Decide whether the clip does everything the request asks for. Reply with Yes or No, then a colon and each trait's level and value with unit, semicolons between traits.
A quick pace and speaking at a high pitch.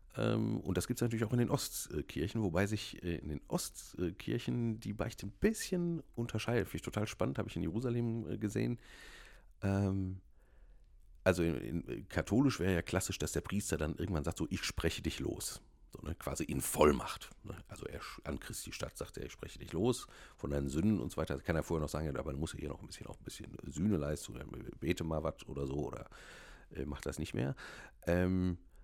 No: fast, 205 wpm; very low, 95 Hz